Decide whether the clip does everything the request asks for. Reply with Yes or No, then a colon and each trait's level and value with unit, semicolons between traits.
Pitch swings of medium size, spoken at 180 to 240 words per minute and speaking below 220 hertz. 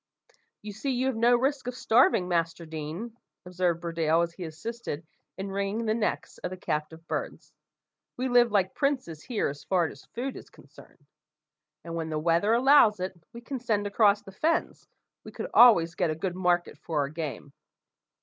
No: wide, 6.0 semitones; average, 190 wpm; high, 190 Hz